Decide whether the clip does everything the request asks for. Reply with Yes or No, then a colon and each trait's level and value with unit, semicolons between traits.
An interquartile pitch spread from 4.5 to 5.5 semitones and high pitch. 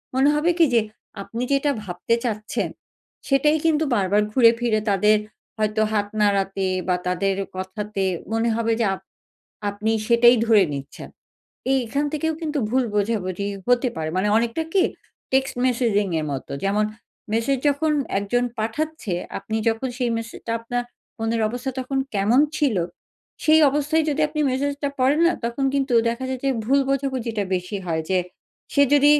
Yes: average, 4.8 semitones; high, 235 Hz